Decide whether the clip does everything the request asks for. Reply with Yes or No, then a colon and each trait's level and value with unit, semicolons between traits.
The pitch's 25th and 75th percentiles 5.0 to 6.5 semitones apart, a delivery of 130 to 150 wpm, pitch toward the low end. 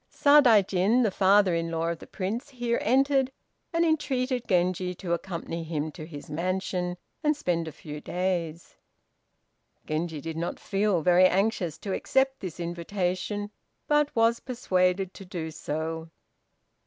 No: average, 5.3 semitones; average, 140 wpm; medium, 185 Hz